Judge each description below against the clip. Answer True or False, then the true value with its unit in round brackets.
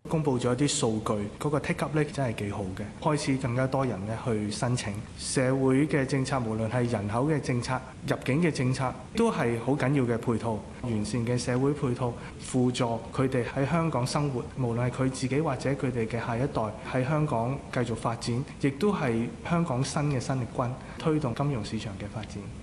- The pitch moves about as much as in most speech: True (3.3 semitones)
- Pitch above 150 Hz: False (130 Hz)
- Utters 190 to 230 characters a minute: False (295 characters per minute)